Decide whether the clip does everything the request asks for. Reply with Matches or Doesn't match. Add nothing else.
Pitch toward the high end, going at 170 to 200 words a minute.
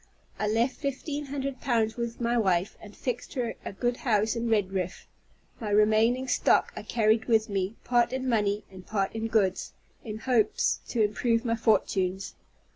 Matches